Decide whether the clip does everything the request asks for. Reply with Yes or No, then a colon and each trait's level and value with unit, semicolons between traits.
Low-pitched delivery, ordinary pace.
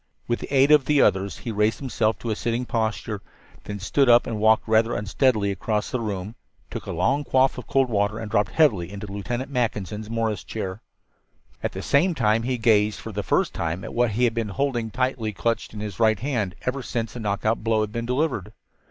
No: low, 110 Hz; fast, 215 wpm